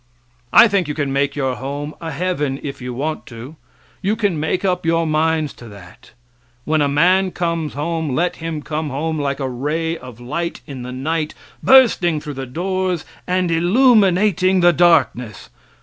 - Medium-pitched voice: Yes, medium, 160 Hz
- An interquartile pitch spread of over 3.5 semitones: Yes, average, 4.1 semitones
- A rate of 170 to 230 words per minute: Yes, average, 175 wpm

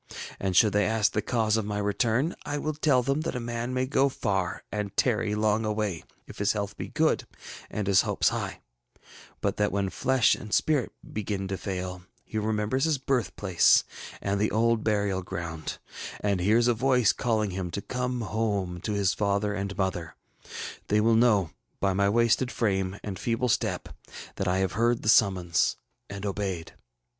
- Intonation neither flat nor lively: Yes, average, 3.2 semitones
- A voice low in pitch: Yes, low, 105 Hz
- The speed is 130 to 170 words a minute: No, average, 185 wpm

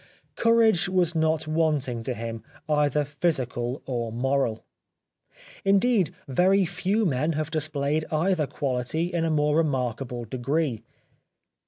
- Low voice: No, medium, 150 Hz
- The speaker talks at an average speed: No, slow, 120 wpm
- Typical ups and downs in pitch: Yes, average, 4.6 semitones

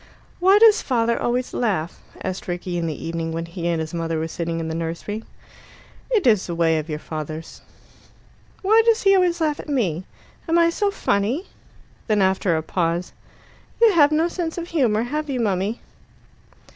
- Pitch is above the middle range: Yes, high, 205 Hz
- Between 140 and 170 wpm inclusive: No, average, 185 wpm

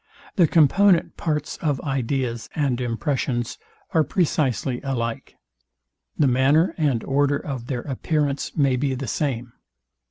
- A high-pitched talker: No, low, 135 Hz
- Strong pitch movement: No, average, 3.3 semitones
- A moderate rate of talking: No, slow, 125 wpm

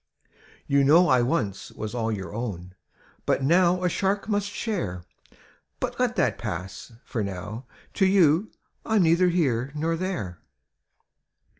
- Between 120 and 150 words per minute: Yes, average, 145 wpm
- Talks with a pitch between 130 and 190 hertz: Yes, medium, 140 Hz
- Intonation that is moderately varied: No, wide, 9.0 semitones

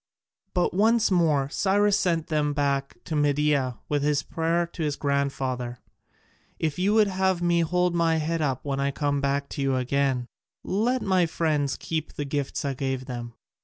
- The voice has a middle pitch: Yes, medium, 150 Hz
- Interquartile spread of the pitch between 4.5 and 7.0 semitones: No, average, 3.8 semitones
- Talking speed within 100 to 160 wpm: No, average, 175 wpm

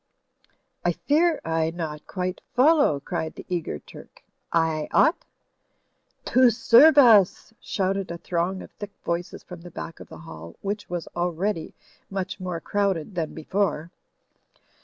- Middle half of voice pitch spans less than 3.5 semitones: No, average, 3.9 semitones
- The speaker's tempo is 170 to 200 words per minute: No, average, 140 wpm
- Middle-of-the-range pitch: Yes, medium, 180 Hz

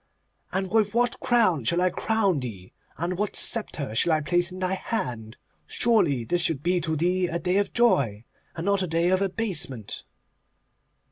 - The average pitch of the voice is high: No, medium, 180 Hz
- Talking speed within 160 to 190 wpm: Yes, average, 180 wpm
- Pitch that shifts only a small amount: No, average, 4.6 semitones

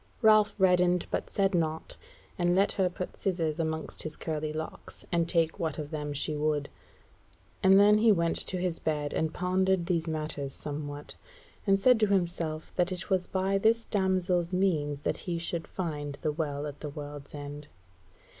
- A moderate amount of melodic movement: Yes, average, 3.8 semitones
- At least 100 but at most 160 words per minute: No, average, 175 wpm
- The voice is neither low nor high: Yes, medium, 170 Hz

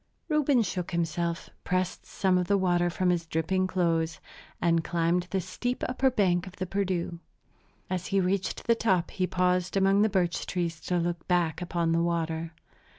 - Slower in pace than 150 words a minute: No, average, 175 wpm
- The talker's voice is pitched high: No, medium, 180 Hz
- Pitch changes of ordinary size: No, narrow, 2.0 semitones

